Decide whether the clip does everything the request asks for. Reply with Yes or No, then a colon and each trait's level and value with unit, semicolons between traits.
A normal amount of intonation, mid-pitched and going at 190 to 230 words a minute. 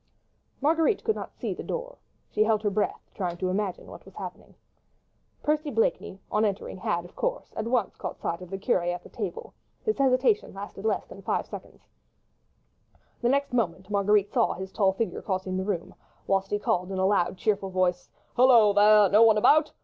No: average, 4.1 semitones; high, 205 Hz; average, 195 wpm